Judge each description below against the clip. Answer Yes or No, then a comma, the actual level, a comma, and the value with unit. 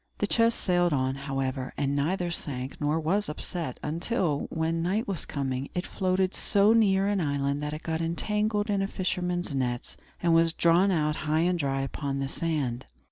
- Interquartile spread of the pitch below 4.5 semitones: No, average, 4.8 semitones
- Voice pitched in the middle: Yes, medium, 165 Hz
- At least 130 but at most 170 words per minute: No, average, 185 wpm